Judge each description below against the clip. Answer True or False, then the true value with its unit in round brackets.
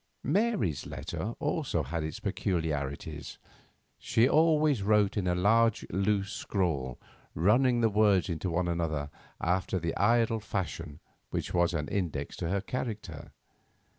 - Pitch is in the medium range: False (95 Hz)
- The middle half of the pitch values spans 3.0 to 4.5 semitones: False (5.1 semitones)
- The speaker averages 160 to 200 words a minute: False (135 wpm)